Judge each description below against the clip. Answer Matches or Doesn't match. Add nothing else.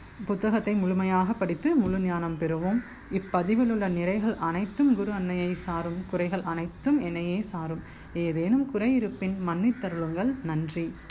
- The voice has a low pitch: Doesn't match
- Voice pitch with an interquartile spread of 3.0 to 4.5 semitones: Matches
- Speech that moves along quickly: Doesn't match